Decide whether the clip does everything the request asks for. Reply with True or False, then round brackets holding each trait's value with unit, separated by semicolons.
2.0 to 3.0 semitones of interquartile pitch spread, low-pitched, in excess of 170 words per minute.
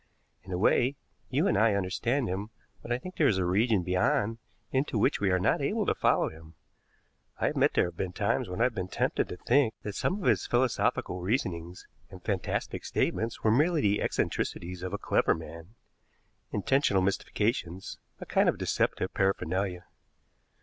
False (4.4 semitones; 100 Hz; 180 wpm)